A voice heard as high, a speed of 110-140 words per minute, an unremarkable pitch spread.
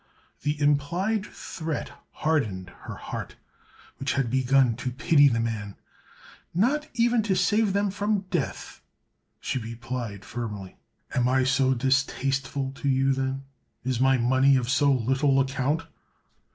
No: low, 135 Hz; slow, 135 wpm; average, 3.4 semitones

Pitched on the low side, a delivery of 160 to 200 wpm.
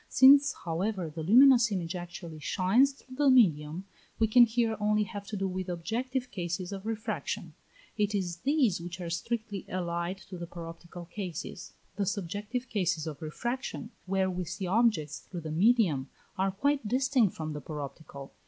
No: high, 190 Hz; average, 165 wpm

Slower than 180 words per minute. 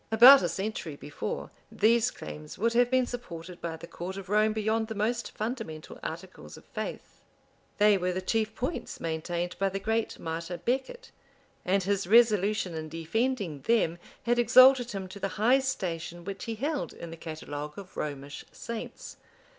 Yes: average, 170 wpm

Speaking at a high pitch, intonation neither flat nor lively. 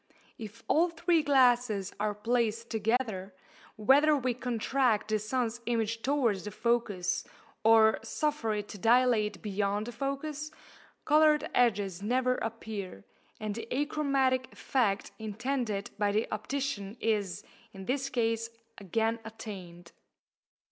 Yes: high, 225 Hz; average, 3.6 semitones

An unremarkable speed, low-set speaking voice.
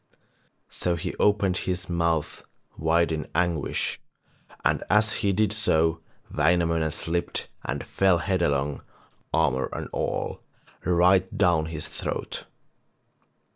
No: slow, 110 wpm; very low, 85 Hz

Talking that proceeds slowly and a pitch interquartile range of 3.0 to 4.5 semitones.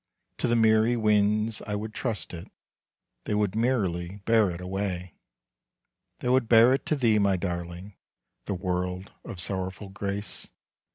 No: average, 150 wpm; average, 3.3 semitones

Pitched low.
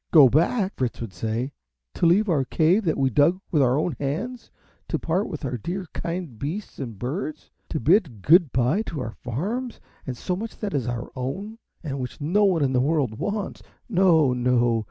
No: medium, 150 Hz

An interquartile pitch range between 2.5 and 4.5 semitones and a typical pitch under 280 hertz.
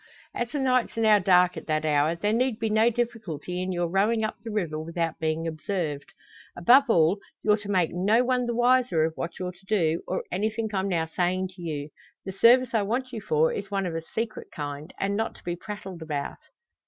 No: average, 5.2 semitones; high, 190 Hz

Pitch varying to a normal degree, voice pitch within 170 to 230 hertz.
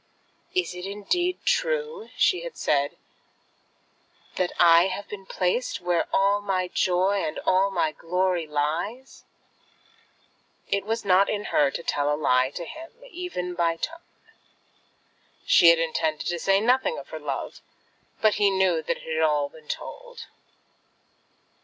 Yes: average, 4.7 semitones; medium, 185 Hz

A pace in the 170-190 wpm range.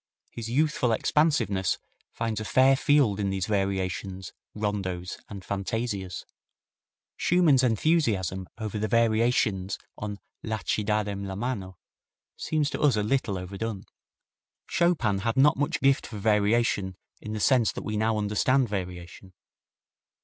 No: slow, 135 wpm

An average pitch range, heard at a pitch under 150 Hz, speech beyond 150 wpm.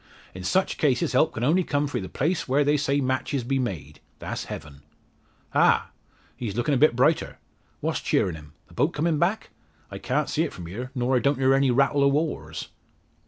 Yes: average, 3.9 semitones; low, 135 Hz; fast, 205 wpm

